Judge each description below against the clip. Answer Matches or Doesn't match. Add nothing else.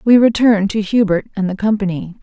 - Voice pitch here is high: Matches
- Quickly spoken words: Doesn't match